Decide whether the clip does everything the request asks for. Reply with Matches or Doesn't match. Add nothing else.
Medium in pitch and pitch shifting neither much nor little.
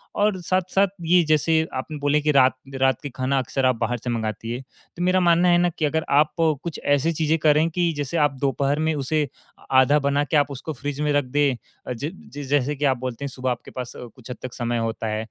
Matches